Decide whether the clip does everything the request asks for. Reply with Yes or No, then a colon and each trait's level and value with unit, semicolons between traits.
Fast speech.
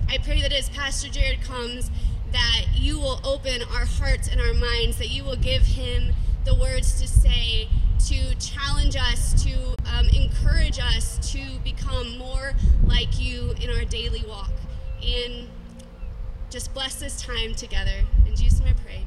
No: average, 165 wpm